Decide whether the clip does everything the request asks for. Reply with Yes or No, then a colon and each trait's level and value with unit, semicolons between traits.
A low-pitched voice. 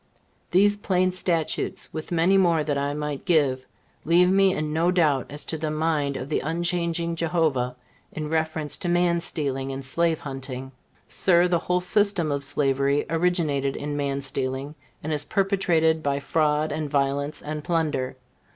No: medium, 155 Hz